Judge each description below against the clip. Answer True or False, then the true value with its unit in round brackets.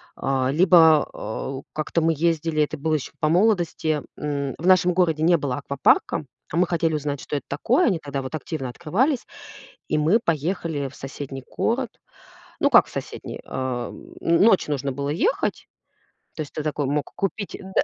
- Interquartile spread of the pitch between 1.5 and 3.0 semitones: False (3.4 semitones)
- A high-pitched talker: False (155 Hz)